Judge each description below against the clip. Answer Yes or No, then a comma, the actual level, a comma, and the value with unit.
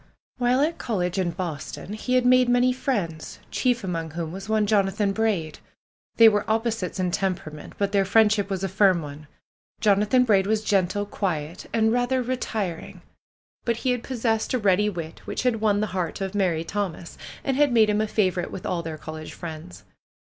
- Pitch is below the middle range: No, high, 205 Hz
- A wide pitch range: No, average, 4.1 semitones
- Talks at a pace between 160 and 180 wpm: No, average, 190 wpm